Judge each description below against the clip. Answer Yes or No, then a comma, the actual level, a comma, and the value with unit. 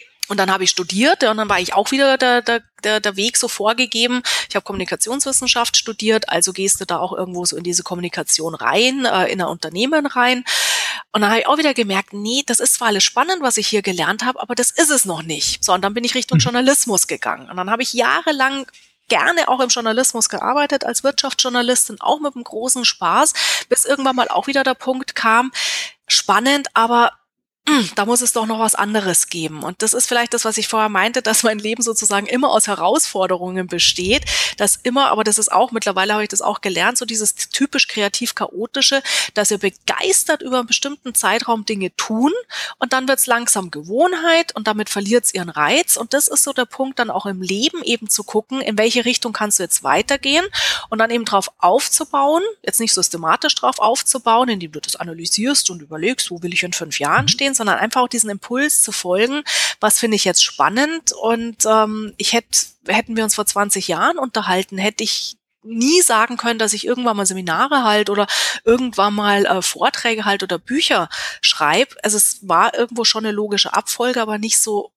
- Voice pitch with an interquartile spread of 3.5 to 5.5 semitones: Yes, average, 4.2 semitones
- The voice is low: No, high, 225 Hz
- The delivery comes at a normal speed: No, fast, 205 wpm